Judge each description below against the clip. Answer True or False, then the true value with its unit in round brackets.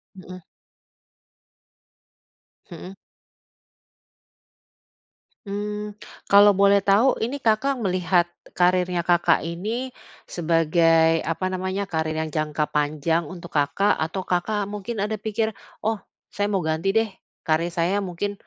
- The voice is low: False (185 Hz)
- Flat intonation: False (3.6 semitones)